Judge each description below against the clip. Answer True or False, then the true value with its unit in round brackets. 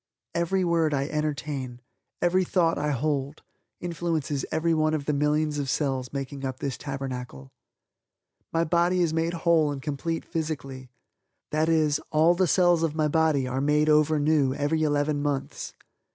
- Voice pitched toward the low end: False (150 Hz)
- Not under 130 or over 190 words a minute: True (155 wpm)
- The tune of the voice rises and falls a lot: False (2.7 semitones)